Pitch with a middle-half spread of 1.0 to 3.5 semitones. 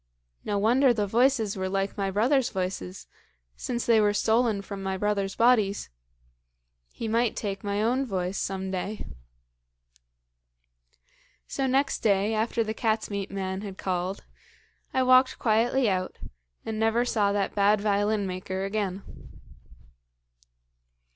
Yes: average, 2.9 semitones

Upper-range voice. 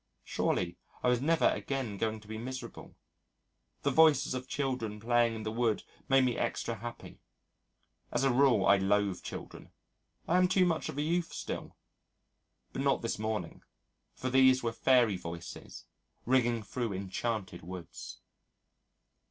No: low, 120 Hz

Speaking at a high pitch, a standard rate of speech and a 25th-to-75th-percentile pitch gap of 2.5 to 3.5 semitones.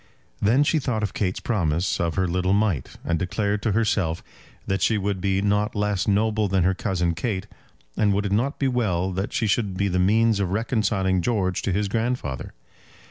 No: low, 100 Hz; average, 195 wpm; average, 2.8 semitones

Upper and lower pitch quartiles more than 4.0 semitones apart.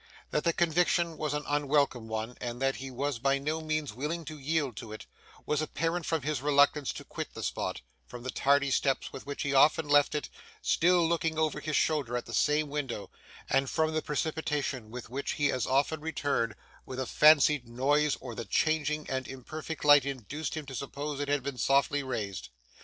No: average, 2.7 semitones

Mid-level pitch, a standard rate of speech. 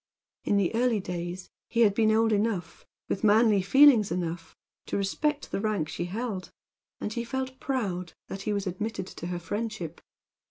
No: high, 205 Hz; average, 175 wpm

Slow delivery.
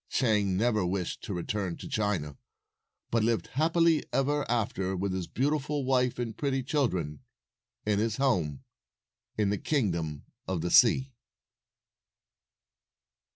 Yes: slow, 125 wpm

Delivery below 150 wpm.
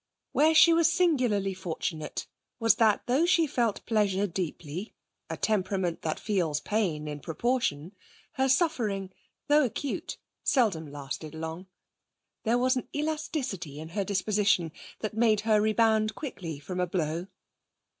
Yes: slow, 135 wpm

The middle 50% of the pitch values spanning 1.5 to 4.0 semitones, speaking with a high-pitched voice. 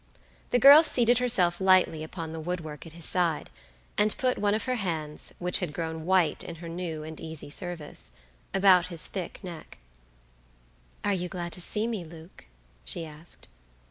No: average, 3.3 semitones; medium, 175 Hz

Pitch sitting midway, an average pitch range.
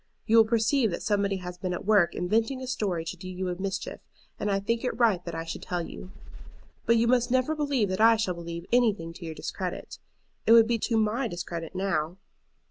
No: high, 200 Hz; average, 4.5 semitones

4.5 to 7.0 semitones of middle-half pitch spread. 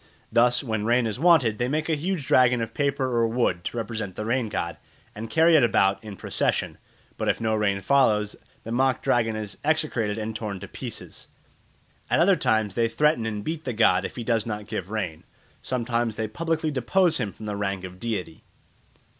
No: average, 3.7 semitones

